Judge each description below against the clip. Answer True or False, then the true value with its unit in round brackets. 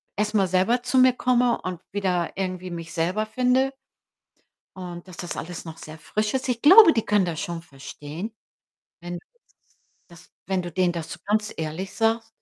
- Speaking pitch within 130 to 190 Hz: True (185 Hz)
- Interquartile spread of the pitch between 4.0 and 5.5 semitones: True (4.7 semitones)